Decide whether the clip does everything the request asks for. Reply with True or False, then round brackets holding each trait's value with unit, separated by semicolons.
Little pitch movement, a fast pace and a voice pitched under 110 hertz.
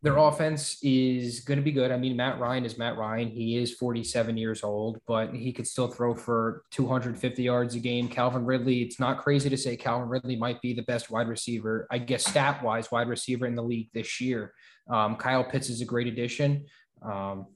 False (1.8 semitones; 210 wpm; 120 Hz)